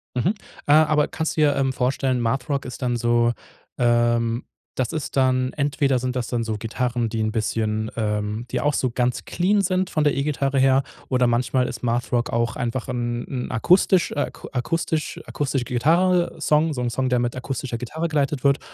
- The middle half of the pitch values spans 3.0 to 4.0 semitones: Yes, average, 3.4 semitones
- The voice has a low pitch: Yes, low, 125 Hz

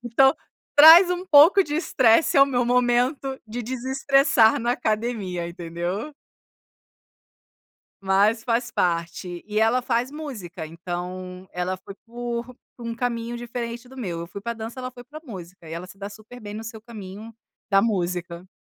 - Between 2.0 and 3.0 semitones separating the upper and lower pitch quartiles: No, average, 5.1 semitones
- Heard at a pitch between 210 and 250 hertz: Yes, high, 230 Hz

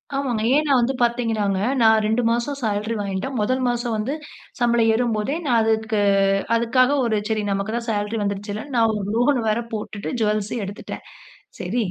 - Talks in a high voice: Yes, high, 225 Hz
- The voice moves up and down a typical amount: No, narrow, 2.3 semitones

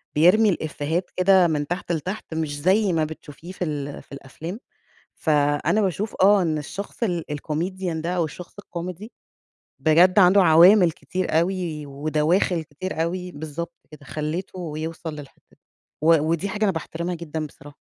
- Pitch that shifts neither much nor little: Yes, average, 3.2 semitones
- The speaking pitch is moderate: Yes, medium, 165 Hz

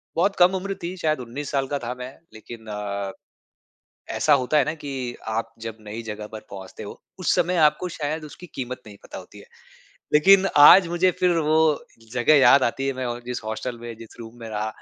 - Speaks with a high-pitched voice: No, low, 130 Hz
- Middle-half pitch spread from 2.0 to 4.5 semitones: No, wide, 5.6 semitones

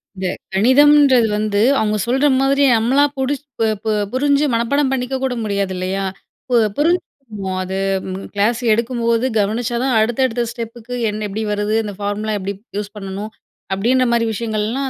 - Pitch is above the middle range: Yes, high, 230 Hz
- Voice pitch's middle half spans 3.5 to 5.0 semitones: Yes, average, 3.9 semitones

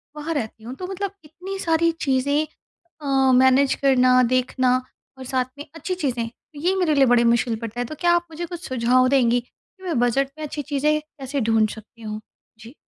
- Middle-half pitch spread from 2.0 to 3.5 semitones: No, average, 4.2 semitones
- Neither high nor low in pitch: No, very high, 270 Hz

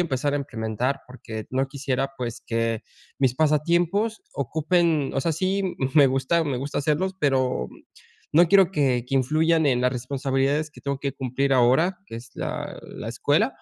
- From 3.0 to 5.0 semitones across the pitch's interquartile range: Yes, average, 3.7 semitones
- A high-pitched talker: No, medium, 140 Hz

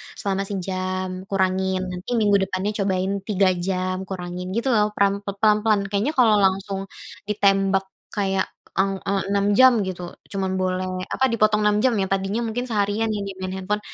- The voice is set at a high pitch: Yes, high, 195 Hz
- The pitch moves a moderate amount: No, narrow, 1.8 semitones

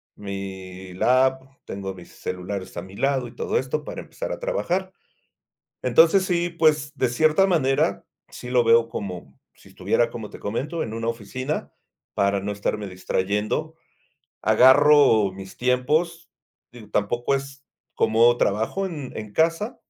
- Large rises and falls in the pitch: Yes, wide, 6.9 semitones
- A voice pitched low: Yes, low, 120 Hz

